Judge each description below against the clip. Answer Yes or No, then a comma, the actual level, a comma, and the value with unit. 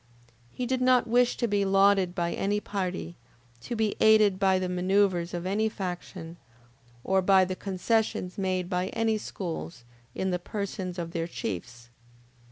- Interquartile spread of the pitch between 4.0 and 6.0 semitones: No, narrow, 2.5 semitones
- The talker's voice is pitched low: No, high, 190 Hz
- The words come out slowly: No, average, 160 wpm